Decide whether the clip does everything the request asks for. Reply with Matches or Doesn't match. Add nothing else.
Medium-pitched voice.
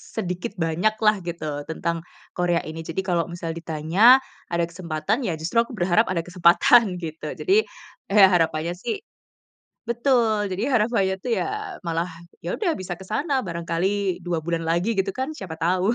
Matches